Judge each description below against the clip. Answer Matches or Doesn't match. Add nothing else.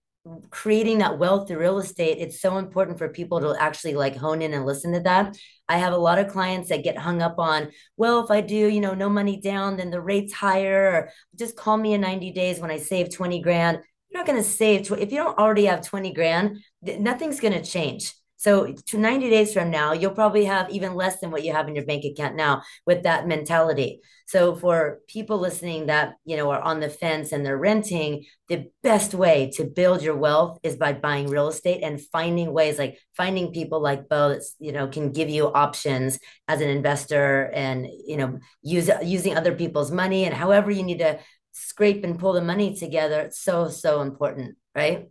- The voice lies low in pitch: Doesn't match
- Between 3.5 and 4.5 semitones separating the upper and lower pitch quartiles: Matches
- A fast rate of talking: Matches